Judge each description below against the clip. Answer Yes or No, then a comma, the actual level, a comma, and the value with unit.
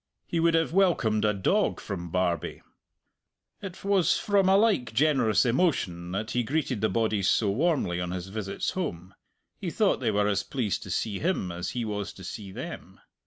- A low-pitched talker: Yes, low, 110 Hz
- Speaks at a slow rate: No, average, 185 wpm